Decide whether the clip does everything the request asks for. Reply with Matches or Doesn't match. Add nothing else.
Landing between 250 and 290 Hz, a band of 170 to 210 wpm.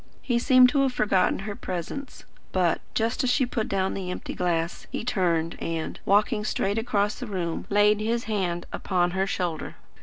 Doesn't match